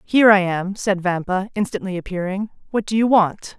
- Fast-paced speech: No, average, 185 wpm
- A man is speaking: No, female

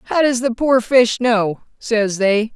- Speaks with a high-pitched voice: Yes, high, 235 Hz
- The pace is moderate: Yes, average, 190 wpm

